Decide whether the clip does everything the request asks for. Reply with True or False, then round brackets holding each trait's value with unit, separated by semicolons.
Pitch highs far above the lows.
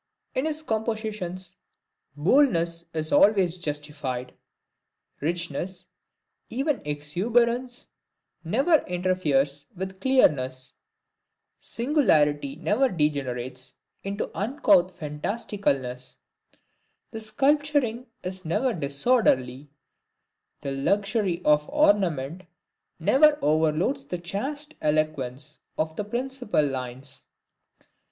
True (7.9 semitones)